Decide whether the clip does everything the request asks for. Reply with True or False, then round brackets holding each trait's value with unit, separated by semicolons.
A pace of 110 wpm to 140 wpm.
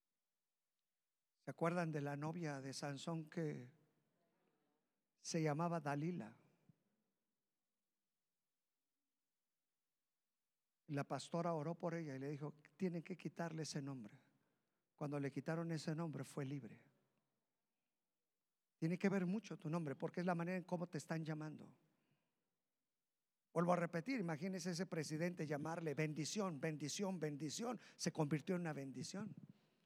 True (125 wpm)